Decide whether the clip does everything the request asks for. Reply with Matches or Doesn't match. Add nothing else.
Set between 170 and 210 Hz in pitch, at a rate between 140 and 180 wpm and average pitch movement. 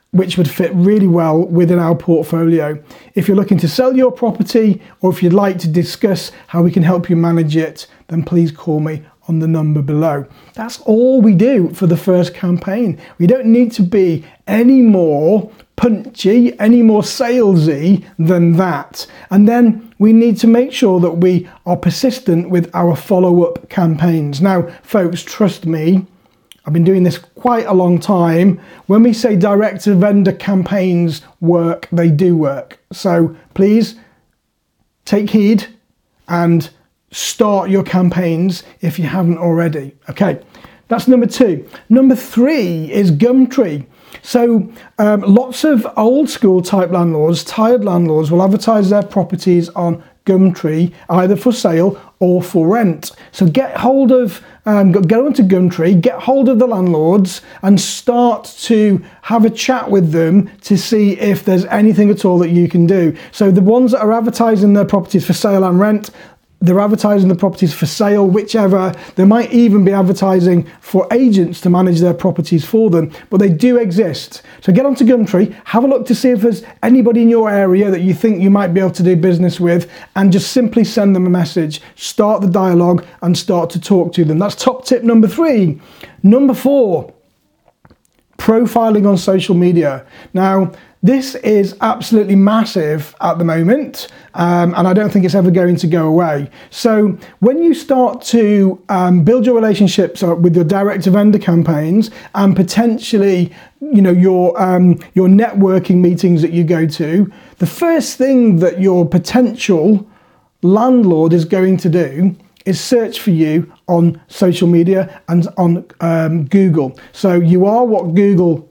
Matches